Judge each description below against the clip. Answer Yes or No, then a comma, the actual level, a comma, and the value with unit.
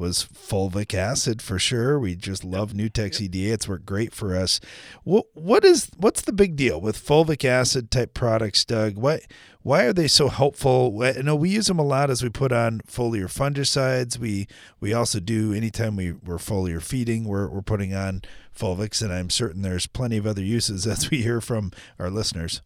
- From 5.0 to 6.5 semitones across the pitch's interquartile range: No, average, 4.5 semitones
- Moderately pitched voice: No, low, 110 Hz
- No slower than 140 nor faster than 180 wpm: No, average, 200 wpm